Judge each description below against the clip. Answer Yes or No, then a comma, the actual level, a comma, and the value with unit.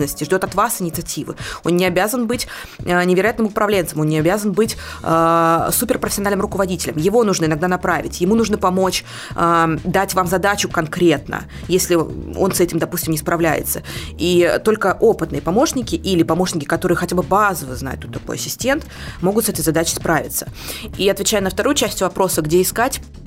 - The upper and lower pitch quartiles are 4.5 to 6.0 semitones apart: No, average, 3.5 semitones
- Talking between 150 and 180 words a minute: Yes, fast, 160 wpm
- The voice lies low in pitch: No, medium, 185 Hz